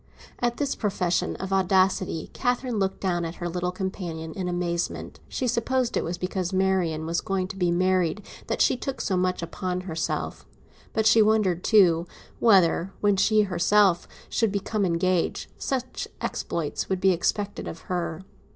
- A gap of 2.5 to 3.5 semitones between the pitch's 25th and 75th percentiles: Yes, average, 2.9 semitones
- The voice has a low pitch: No, medium, 185 Hz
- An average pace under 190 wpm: Yes, average, 160 wpm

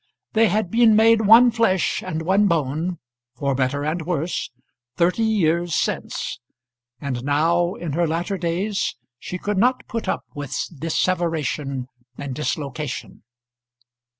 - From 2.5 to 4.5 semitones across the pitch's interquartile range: No, wide, 5.6 semitones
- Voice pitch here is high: No, medium, 170 Hz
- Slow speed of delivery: Yes, slow, 130 wpm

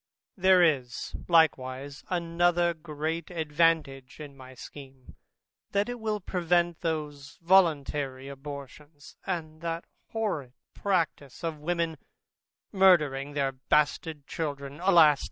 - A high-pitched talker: No, medium, 155 Hz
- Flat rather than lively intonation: No, average, 3.6 semitones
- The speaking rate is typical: No, slow, 105 wpm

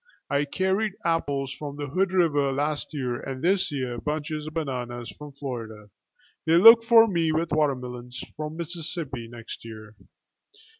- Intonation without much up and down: No, average, 4.7 semitones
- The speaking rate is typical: Yes, average, 150 wpm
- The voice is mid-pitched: Yes, medium, 145 Hz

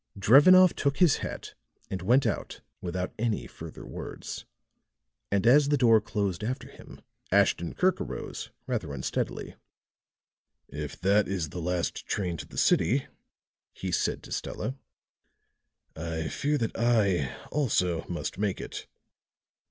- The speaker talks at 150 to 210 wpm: No, slow, 135 wpm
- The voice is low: Yes, low, 100 Hz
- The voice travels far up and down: Yes, wide, 6.3 semitones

